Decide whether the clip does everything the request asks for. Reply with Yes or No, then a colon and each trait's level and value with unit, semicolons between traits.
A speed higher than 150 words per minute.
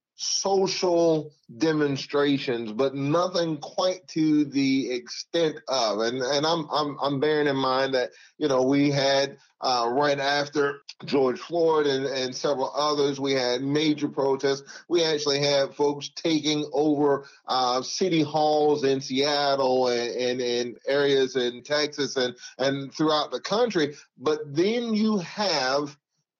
No: slow, 135 wpm